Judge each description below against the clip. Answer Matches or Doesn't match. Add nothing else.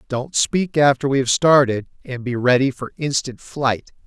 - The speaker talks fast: Doesn't match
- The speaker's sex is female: Doesn't match